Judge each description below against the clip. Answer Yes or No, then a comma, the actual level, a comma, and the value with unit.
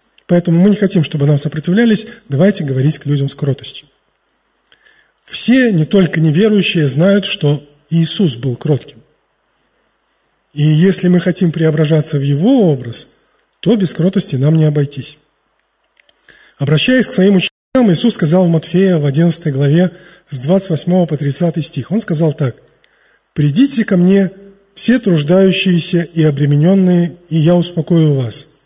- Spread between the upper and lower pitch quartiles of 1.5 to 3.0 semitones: No, average, 4.3 semitones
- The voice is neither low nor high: Yes, medium, 165 Hz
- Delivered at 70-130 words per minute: No, average, 140 wpm